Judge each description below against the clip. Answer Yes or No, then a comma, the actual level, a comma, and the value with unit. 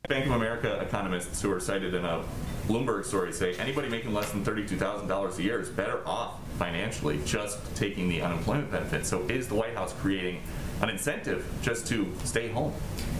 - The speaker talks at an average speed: Yes, average, 180 wpm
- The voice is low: Yes, low, 100 Hz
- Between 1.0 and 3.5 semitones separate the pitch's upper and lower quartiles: No, average, 4.2 semitones